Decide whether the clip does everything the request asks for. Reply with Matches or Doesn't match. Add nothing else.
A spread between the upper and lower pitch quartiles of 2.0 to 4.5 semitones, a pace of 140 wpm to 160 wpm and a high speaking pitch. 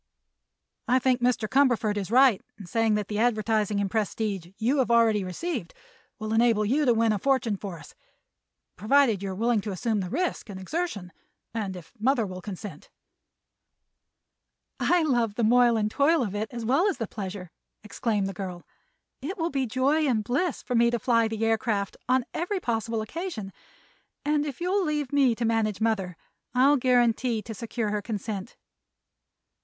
Doesn't match